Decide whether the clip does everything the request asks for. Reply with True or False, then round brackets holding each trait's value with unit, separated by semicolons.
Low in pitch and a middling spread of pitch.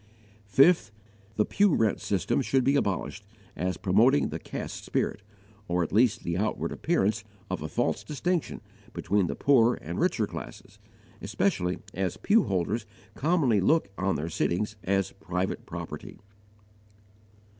False (105 Hz; 6.4 semitones)